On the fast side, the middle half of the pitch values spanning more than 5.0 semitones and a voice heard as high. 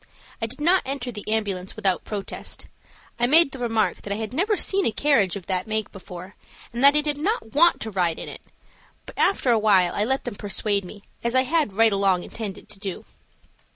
Yes: fast, 215 wpm; wide, 5.5 semitones; high, 220 Hz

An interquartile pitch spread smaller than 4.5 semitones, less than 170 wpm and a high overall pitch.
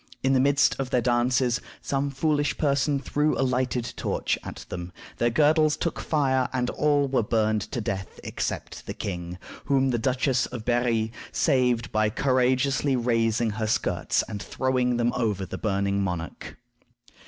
No: average, 3.4 semitones; average, 160 wpm; low, 125 Hz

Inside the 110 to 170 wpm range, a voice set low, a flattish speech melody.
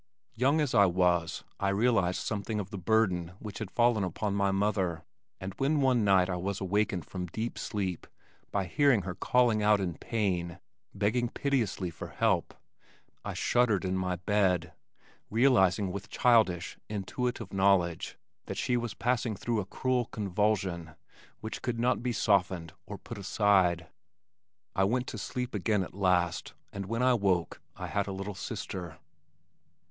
No: average, 160 wpm; low, 100 Hz; average, 3.7 semitones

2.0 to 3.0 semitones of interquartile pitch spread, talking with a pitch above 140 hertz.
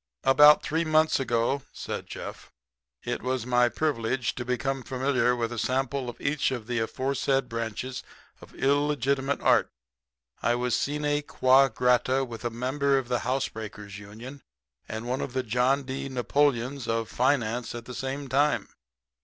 No: narrow, 2.5 semitones; low, 130 Hz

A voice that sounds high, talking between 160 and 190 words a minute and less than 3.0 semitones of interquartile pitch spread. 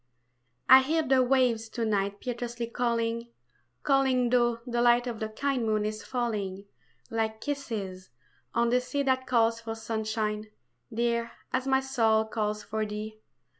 No: high, 235 Hz; average, 150 wpm; narrow, 2.5 semitones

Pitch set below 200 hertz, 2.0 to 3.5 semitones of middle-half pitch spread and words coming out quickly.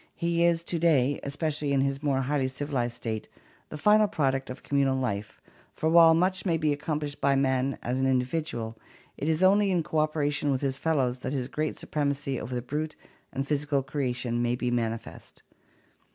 No: medium, 140 Hz; average, 3.1 semitones; average, 185 wpm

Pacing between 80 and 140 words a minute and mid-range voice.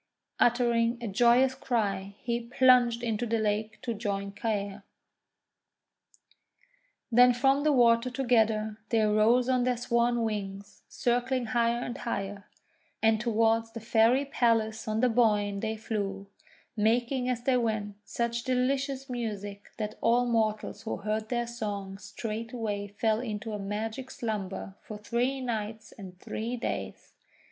No: slow, 135 wpm; high, 225 Hz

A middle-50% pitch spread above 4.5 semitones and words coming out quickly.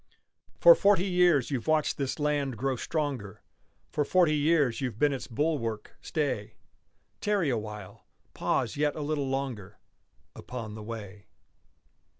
No: average, 5.1 semitones; slow, 135 wpm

